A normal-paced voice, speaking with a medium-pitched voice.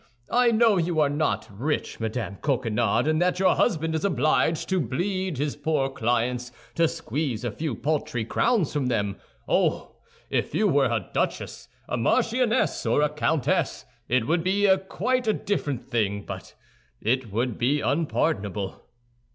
Yes: average, 150 wpm; medium, 145 Hz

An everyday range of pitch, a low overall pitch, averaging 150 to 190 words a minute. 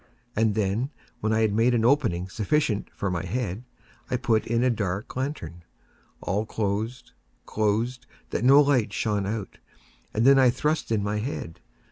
Yes: average, 3.5 semitones; low, 110 Hz; average, 165 wpm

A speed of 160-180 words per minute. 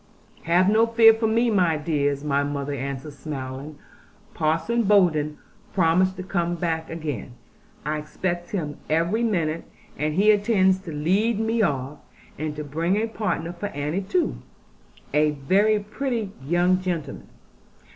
No: average, 145 wpm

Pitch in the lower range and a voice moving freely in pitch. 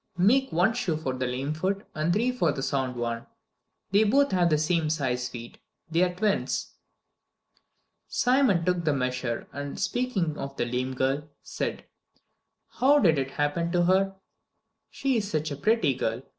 No: medium, 160 Hz; wide, 6.7 semitones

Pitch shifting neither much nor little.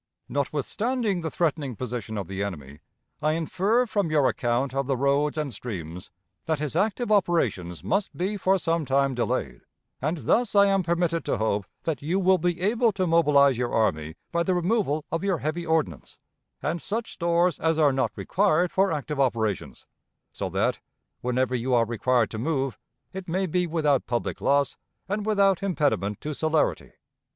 No: wide, 6.2 semitones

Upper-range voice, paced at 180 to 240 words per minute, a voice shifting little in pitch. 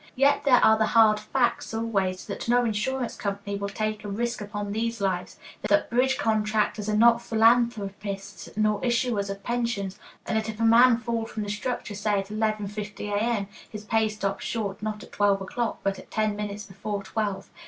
Yes: high, 215 Hz; average, 185 wpm; narrow, 2.2 semitones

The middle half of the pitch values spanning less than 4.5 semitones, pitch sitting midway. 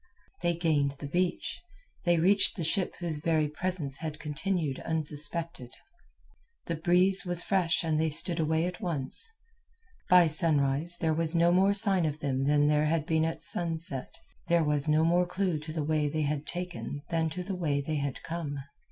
Yes: average, 2.7 semitones; medium, 160 Hz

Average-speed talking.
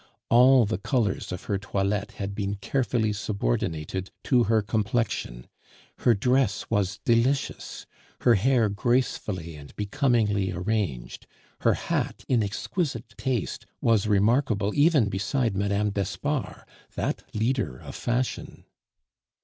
No: slow, 115 wpm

